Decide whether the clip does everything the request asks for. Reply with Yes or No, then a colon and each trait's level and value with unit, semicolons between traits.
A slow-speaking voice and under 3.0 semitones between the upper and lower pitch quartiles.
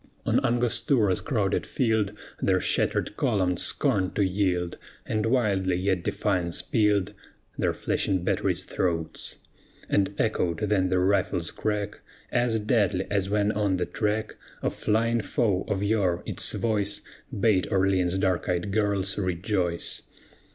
Yes: slow, 130 wpm; narrow, 2.6 semitones